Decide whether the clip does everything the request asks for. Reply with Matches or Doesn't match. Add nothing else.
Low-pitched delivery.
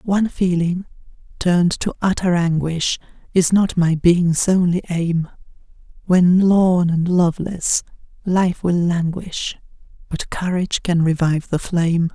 Doesn't match